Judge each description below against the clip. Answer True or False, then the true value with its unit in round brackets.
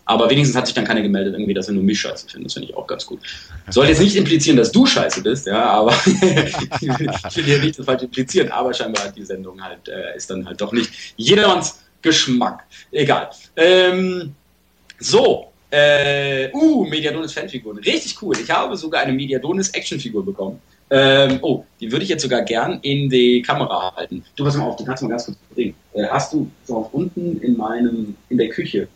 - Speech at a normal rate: True (195 wpm)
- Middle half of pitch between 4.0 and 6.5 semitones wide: True (5.4 semitones)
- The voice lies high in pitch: False (135 Hz)